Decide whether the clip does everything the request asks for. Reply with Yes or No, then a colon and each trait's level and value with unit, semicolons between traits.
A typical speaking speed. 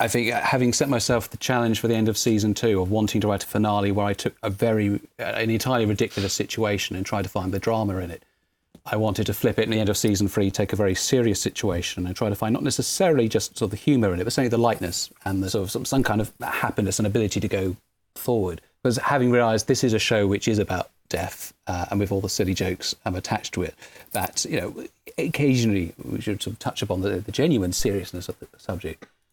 No: fast, 250 wpm